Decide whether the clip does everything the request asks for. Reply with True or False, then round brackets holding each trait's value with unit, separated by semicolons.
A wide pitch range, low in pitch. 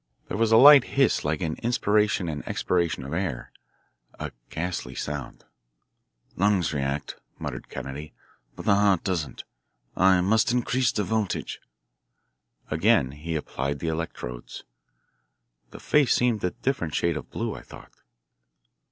True (6.5 semitones; 90 Hz)